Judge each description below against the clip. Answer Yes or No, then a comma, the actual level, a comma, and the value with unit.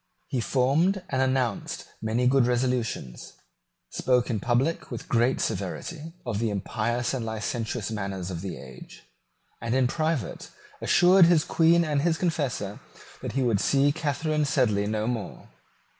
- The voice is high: No, low, 125 Hz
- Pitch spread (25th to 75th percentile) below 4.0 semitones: No, average, 5.2 semitones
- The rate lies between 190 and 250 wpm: No, average, 145 wpm